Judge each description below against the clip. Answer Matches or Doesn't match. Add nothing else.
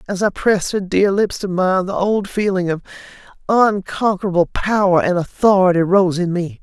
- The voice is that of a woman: Matches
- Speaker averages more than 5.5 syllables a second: Doesn't match